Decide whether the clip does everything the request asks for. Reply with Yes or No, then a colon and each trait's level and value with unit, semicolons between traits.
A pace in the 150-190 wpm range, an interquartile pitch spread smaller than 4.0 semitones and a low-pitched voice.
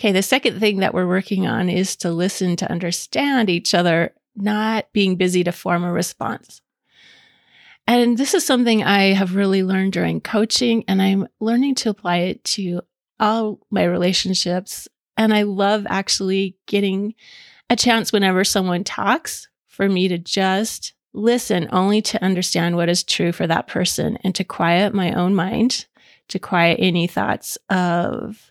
No: average, 160 wpm; average, 3.1 semitones; high, 195 Hz